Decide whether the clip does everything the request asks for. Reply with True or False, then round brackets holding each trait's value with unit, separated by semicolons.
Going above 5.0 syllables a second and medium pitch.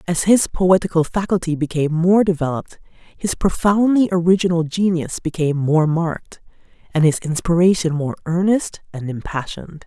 True (5.3 syllables/s; 170 Hz)